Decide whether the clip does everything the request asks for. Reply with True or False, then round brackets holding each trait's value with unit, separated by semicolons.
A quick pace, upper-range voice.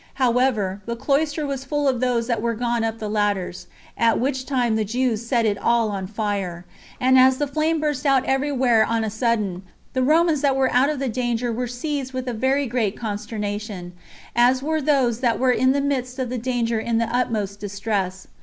True (210 wpm; 240 Hz)